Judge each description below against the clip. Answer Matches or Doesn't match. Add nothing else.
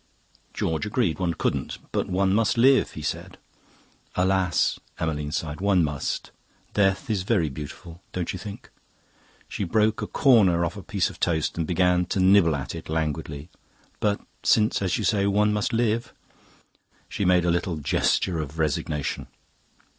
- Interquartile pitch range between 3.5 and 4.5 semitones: Matches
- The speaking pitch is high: Doesn't match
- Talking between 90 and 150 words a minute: Doesn't match